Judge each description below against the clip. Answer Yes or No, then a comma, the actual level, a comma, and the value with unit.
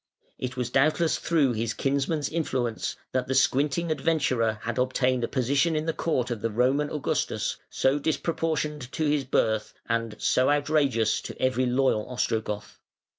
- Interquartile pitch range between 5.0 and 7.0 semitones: No, average, 3.7 semitones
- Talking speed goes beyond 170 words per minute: No, average, 155 wpm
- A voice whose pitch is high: No, low, 130 Hz